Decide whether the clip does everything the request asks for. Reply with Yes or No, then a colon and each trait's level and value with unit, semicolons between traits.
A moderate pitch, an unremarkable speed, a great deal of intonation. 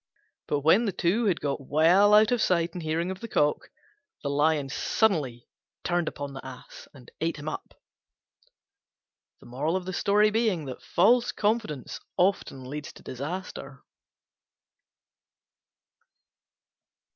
No: medium, 165 Hz; slow, 110 wpm; wide, 5.8 semitones